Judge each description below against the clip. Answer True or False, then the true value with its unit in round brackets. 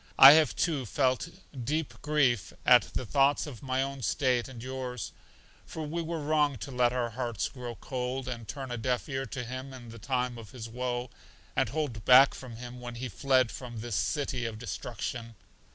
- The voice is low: True (125 Hz)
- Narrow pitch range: True (2.3 semitones)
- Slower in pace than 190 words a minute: False (195 wpm)